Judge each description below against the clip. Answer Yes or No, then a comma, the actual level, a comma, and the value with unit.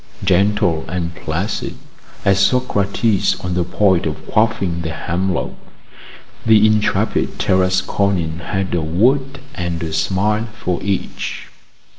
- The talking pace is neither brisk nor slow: No, slow, 115 wpm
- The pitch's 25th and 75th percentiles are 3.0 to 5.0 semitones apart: Yes, average, 3.4 semitones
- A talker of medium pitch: No, very low, 95 Hz